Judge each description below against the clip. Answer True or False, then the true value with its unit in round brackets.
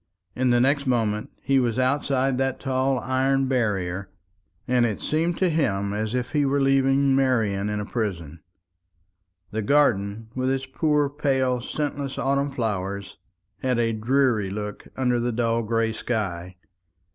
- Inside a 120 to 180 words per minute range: True (150 wpm)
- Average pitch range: True (4.1 semitones)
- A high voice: False (125 Hz)